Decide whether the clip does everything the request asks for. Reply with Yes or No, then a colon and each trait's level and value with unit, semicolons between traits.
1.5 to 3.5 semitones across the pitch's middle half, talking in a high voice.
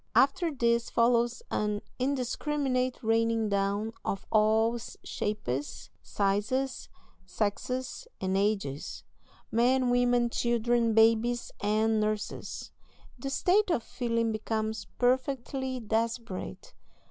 Yes: average, 2.9 semitones; high, 230 Hz